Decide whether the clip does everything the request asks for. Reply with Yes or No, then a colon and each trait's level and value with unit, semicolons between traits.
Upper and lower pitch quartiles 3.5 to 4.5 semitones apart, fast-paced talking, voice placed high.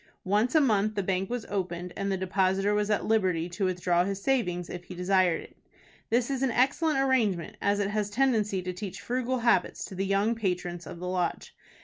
Yes: average, 3.8 semitones; fast, 215 wpm; high, 195 Hz